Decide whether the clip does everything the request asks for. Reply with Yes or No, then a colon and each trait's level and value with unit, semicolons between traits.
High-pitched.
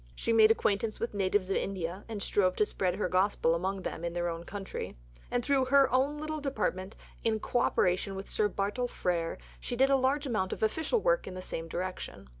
Yes: high, 205 Hz